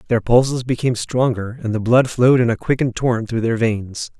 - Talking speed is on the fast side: Yes, fast, 215 wpm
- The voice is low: Yes, low, 120 Hz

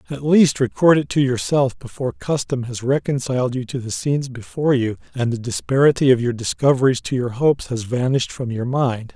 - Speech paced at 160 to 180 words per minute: No, average, 195 wpm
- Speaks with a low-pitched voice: Yes, low, 130 Hz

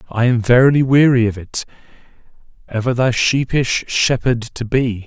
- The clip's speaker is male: Yes, male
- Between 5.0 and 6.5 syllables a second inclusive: No, 4.7 syllables/s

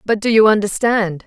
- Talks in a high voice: Yes, high, 210 Hz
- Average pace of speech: Yes, average, 190 wpm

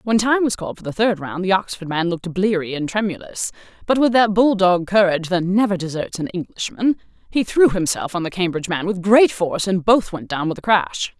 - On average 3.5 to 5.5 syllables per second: No, 5.7 syllables/s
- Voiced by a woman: Yes, female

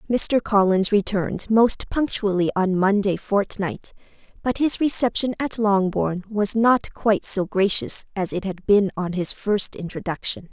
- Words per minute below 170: Yes, average, 150 wpm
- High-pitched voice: Yes, high, 205 Hz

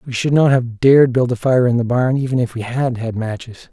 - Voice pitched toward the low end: Yes, low, 125 Hz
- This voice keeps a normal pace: No, fast, 275 wpm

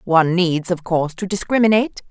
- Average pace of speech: Yes, average, 170 wpm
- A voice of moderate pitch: Yes, medium, 180 Hz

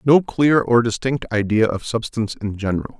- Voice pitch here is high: No, low, 115 Hz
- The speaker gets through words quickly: No, average, 180 wpm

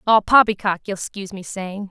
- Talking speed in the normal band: Yes, average, 190 wpm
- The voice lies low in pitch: No, high, 200 Hz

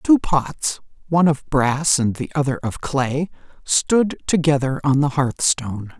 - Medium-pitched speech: Yes, medium, 145 Hz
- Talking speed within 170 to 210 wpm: No, average, 150 wpm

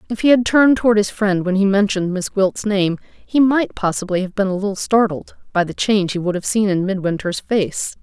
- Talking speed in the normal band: No, fast, 230 wpm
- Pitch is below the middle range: No, high, 200 Hz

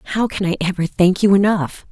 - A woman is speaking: Yes, female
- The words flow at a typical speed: No, fast, 220 wpm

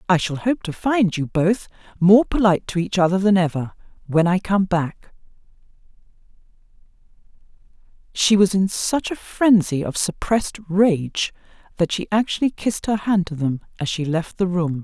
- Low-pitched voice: No, medium, 185 Hz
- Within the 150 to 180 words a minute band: Yes, average, 160 wpm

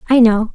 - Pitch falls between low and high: No, high, 230 Hz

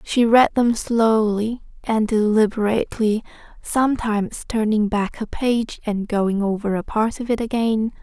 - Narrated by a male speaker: No, female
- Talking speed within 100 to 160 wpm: Yes, average, 140 wpm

